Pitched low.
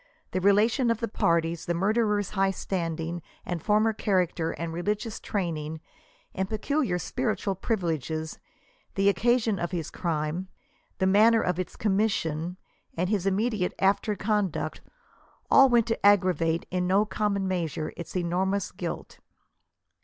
No: high, 190 Hz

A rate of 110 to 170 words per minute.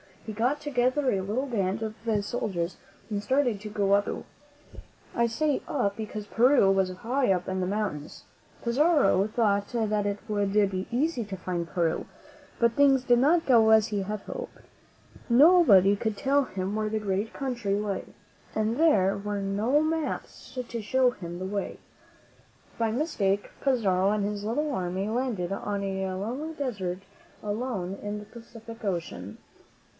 Yes: average, 165 wpm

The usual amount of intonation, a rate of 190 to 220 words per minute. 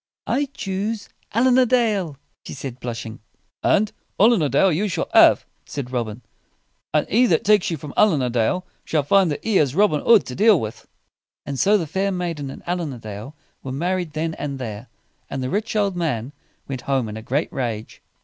No: wide, 7.4 semitones; average, 200 wpm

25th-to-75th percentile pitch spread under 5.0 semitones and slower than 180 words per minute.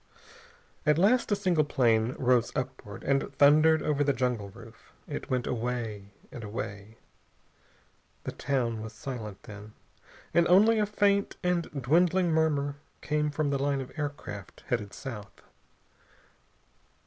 No: wide, 5.6 semitones; slow, 135 wpm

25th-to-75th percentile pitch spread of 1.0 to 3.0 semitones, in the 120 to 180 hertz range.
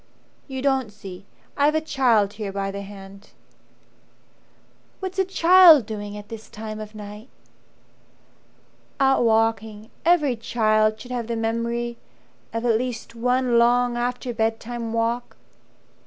No: narrow, 2.6 semitones; high, 230 Hz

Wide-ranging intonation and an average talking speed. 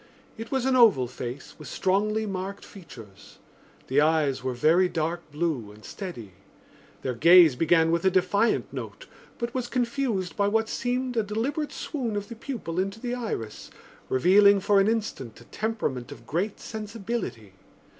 Yes: wide, 6.7 semitones; average, 160 wpm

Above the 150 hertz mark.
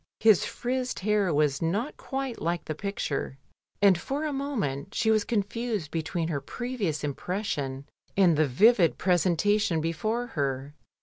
Yes: high, 190 Hz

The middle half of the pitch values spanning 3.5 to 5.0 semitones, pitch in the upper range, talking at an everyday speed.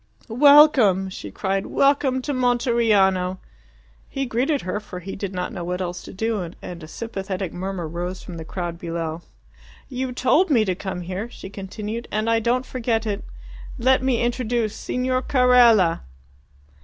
No: wide, 5.4 semitones; high, 215 Hz; average, 160 wpm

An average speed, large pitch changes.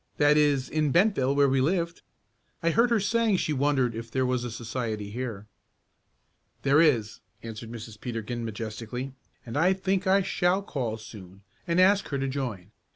Yes: average, 170 wpm; wide, 6.6 semitones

